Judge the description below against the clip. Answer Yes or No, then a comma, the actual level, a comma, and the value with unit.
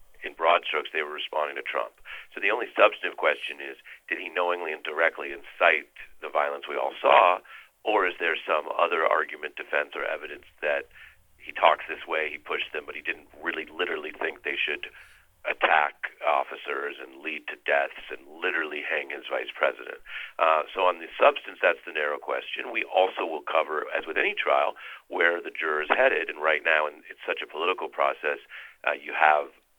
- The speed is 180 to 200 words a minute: Yes, average, 195 wpm